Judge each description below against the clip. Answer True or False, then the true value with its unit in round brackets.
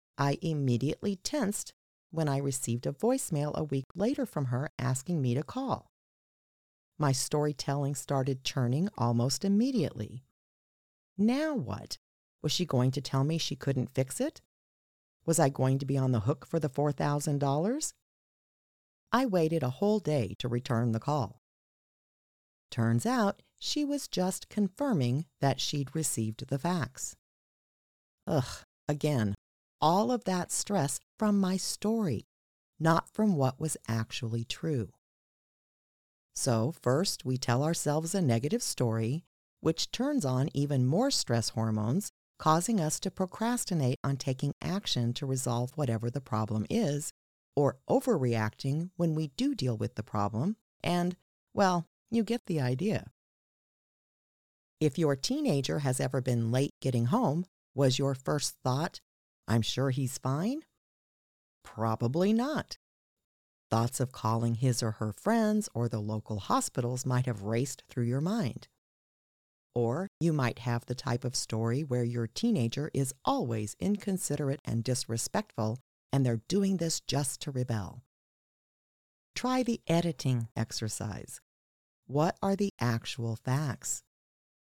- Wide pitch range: True (6.3 semitones)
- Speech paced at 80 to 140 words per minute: True (135 wpm)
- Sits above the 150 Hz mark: False (140 Hz)